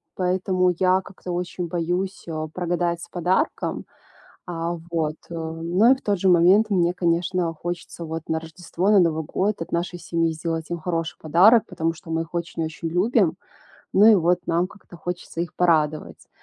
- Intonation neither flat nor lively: No, narrow, 1.8 semitones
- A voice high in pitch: No, medium, 175 Hz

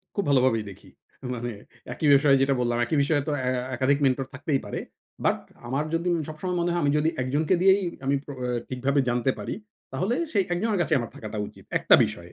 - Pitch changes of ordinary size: Yes, average, 4.5 semitones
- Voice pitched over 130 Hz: Yes, medium, 140 Hz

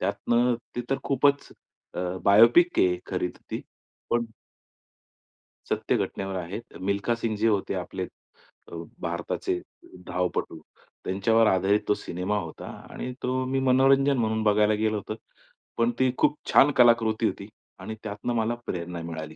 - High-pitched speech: No, low, 110 Hz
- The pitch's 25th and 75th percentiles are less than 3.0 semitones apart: No, average, 4.4 semitones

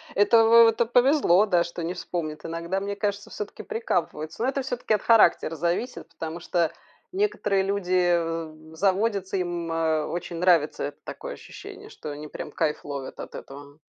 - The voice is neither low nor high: Yes, medium, 180 Hz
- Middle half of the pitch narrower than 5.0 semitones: No, wide, 5.4 semitones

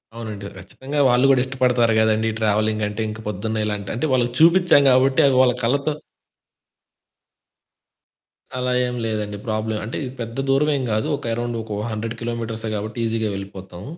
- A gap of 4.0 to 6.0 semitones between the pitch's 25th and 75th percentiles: No, average, 2.9 semitones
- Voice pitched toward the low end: Yes, low, 115 Hz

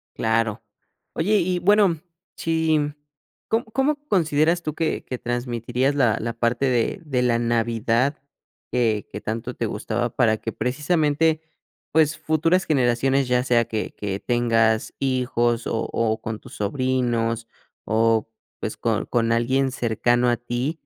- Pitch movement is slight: No, average, 4.7 semitones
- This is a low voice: Yes, low, 125 Hz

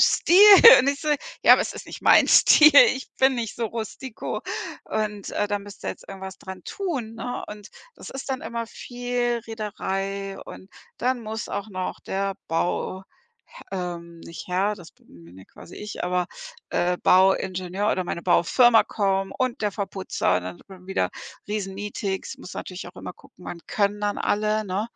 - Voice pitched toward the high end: Yes, high, 200 Hz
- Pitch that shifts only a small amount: No, average, 3.3 semitones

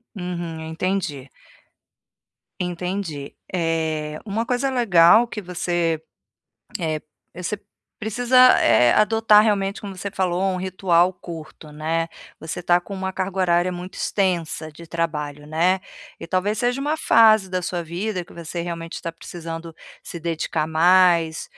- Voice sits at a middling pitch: Yes, medium, 175 Hz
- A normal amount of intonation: Yes, average, 3.0 semitones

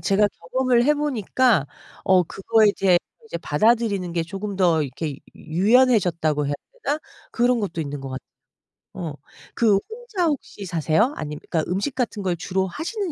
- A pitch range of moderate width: No, wide, 6.6 semitones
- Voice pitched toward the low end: No, high, 195 Hz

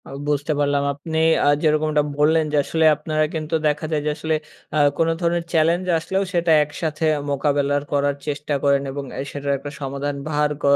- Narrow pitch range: Yes, narrow, 1.9 semitones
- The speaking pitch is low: No, medium, 150 Hz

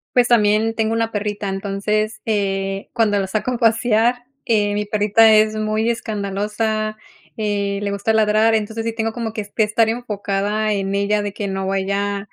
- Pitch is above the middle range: Yes, high, 215 Hz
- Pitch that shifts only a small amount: Yes, narrow, 1.7 semitones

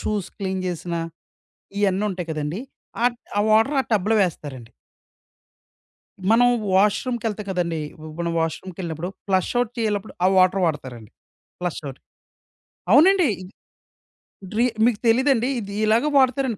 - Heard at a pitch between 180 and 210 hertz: Yes, high, 195 Hz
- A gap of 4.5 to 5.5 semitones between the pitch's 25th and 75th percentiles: Yes, average, 5.1 semitones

